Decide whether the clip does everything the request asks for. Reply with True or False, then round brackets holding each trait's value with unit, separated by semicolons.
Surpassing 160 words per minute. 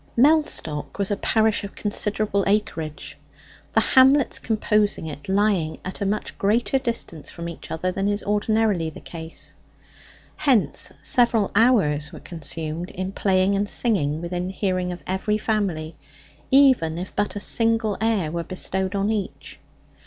False (145 wpm)